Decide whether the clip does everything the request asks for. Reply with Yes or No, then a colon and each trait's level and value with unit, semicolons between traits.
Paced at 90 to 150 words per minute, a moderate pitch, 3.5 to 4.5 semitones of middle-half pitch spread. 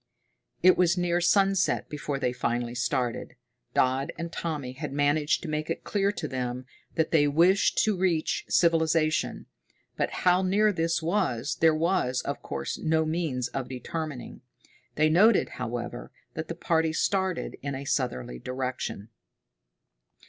No: average, 145 wpm; medium, 155 Hz; average, 5.0 semitones